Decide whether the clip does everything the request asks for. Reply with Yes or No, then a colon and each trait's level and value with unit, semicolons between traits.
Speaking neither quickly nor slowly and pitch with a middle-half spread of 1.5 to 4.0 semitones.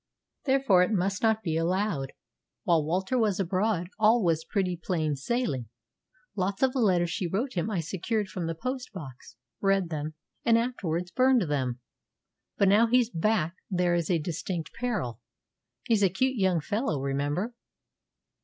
No: average, 160 wpm; average, 5.2 semitones